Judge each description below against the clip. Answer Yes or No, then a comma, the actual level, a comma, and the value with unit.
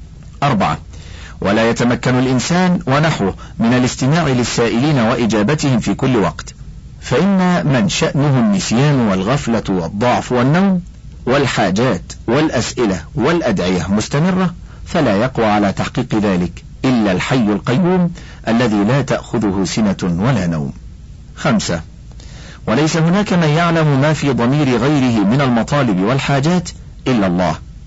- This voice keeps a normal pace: Yes, average, 110 wpm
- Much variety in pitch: Yes, wide, 7.6 semitones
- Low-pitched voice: Yes, low, 130 Hz